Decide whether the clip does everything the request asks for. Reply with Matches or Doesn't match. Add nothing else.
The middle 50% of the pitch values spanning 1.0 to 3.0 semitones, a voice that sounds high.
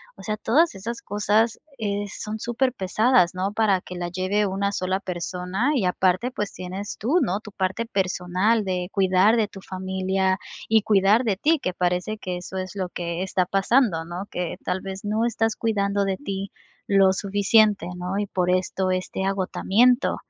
Matches